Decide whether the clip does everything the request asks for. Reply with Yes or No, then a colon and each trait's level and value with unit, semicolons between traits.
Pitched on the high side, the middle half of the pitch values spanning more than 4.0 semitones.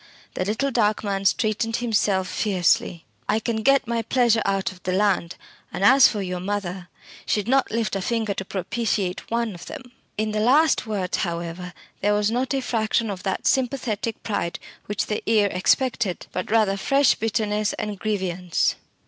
No: high, 210 Hz; average, 3.4 semitones